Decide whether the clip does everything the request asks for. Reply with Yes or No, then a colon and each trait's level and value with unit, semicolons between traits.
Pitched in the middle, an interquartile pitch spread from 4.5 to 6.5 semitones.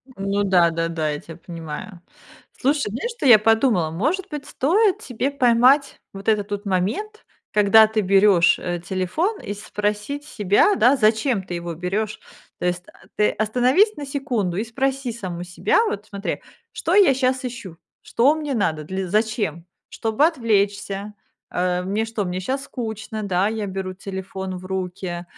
No: high, 210 Hz; average, 5.3 semitones